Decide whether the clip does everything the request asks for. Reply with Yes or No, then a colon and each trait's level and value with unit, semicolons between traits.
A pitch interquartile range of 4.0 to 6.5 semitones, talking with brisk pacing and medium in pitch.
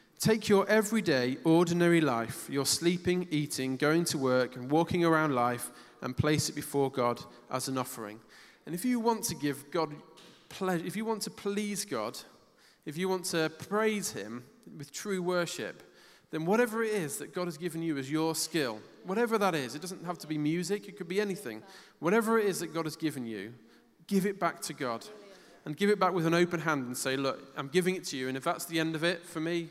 Yes: average, 4.5 semitones; fast, 220 wpm; medium, 165 Hz